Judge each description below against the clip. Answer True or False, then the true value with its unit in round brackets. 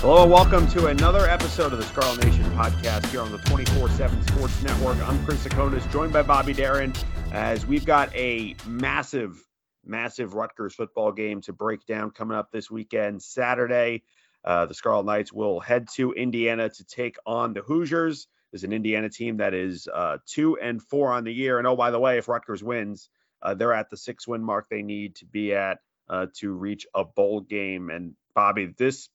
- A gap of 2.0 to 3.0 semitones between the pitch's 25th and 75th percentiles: False (4.1 semitones)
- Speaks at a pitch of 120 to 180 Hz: False (110 Hz)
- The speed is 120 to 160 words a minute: False (200 wpm)